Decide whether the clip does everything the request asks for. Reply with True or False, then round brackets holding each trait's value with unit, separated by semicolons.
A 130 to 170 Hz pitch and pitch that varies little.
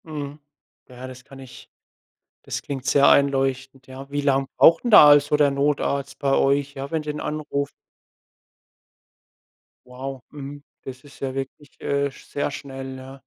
True (140 Hz; 1.3 semitones)